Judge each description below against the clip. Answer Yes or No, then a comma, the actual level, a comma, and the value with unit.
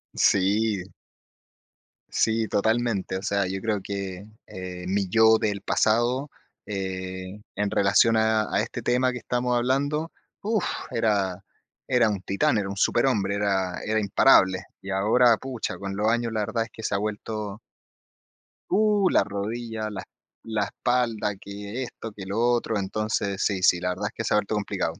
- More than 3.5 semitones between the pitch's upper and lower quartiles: No, average, 2.8 semitones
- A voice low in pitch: Yes, low, 105 Hz